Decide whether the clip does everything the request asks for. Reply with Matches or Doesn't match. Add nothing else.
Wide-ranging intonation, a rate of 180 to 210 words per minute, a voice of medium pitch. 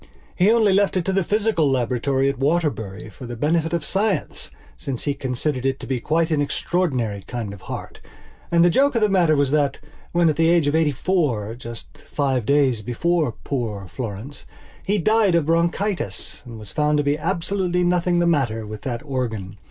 Matches